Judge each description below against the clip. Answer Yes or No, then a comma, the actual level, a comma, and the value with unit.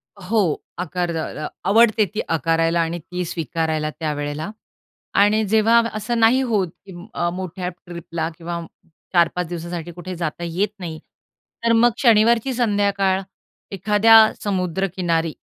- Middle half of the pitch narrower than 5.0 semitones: Yes, average, 4.2 semitones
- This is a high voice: No, medium, 180 Hz